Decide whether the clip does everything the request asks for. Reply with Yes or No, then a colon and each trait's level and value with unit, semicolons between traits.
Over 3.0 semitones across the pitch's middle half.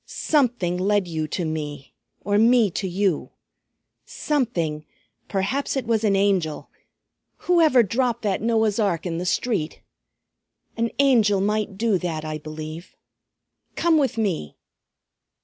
Yes: wide, 5.5 semitones